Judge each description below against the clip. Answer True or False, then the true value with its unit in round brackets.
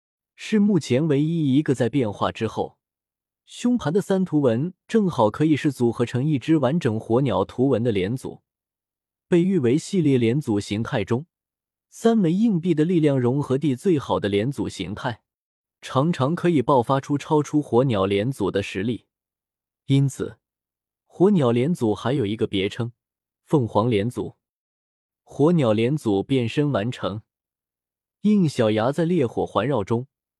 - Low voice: True (130 Hz)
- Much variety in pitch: True (5.8 semitones)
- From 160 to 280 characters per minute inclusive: True (225 characters per minute)